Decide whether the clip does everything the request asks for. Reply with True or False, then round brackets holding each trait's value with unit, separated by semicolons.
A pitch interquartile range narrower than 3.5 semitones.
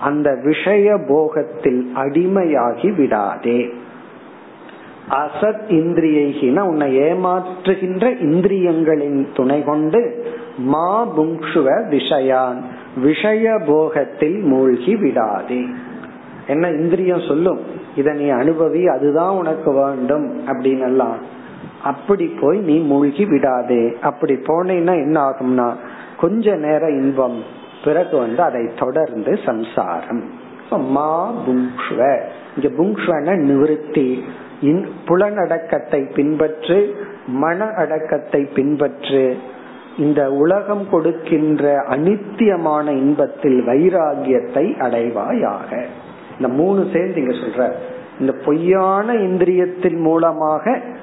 False (4.7 semitones)